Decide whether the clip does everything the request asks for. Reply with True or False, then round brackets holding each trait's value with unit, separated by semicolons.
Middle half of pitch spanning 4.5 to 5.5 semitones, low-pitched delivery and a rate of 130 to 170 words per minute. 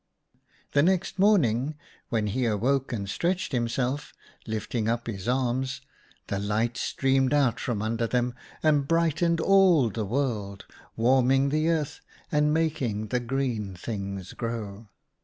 True (4.9 semitones; 125 Hz; 140 wpm)